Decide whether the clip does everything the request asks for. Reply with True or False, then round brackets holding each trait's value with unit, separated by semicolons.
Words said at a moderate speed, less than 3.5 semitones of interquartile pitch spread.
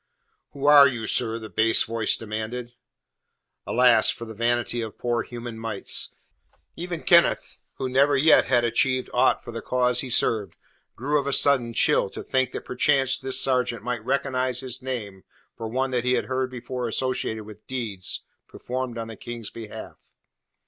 True (170 wpm; 2.4 semitones)